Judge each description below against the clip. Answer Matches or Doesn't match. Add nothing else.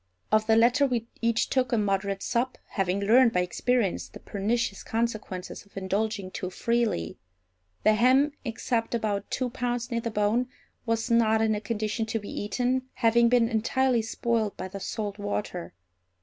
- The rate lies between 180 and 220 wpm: Doesn't match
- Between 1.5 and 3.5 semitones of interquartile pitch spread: Matches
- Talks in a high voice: Matches